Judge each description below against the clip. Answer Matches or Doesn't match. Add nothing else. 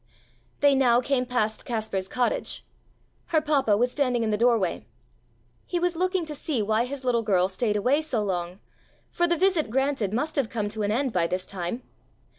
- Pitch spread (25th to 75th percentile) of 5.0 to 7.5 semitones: Matches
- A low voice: Doesn't match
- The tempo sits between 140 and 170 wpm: Doesn't match